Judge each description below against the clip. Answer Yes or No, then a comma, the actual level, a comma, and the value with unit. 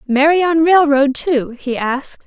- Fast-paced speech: No, average, 160 wpm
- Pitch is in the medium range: No, very high, 290 Hz